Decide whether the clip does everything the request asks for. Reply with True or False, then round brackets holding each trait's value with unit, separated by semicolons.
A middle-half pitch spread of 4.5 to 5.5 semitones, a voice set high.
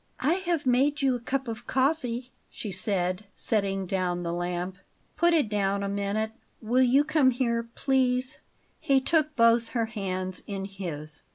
True (5.1 semitones; 230 Hz)